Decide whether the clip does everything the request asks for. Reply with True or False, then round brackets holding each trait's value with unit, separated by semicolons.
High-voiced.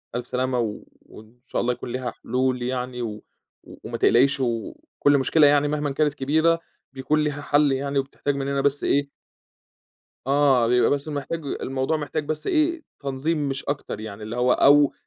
False (140 Hz)